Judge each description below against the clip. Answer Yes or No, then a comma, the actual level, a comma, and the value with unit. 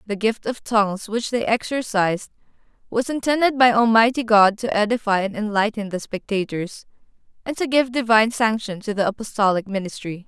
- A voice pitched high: Yes, high, 220 Hz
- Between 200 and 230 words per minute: No, average, 160 wpm